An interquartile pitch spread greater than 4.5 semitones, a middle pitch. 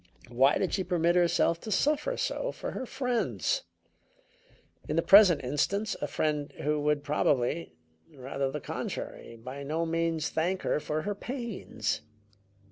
Yes: wide, 5.6 semitones; medium, 165 Hz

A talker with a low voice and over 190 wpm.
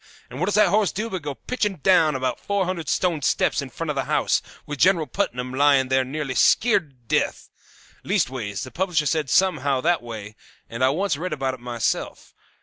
No: medium, 150 Hz; fast, 205 wpm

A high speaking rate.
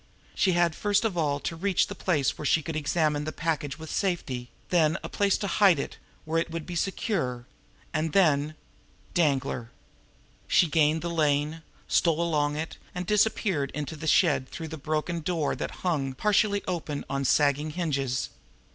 No: average, 175 wpm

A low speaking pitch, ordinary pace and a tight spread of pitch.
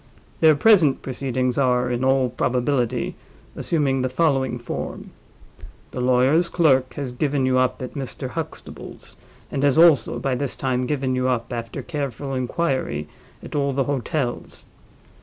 Yes: low, 130 Hz; average, 145 wpm; narrow, 2.2 semitones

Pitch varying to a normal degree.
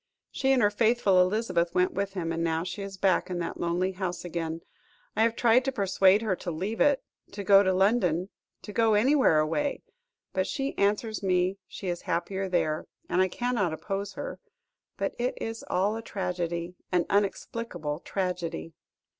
Yes: average, 3.6 semitones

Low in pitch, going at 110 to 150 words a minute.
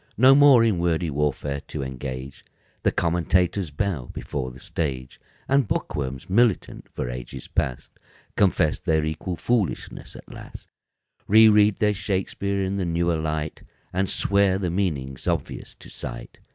Yes: very low, 85 Hz; average, 140 wpm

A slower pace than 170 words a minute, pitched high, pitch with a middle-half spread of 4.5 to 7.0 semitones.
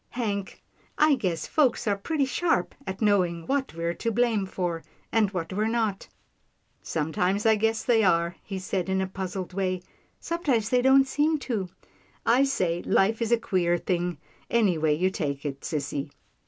No: average, 175 wpm; high, 195 Hz; average, 4.9 semitones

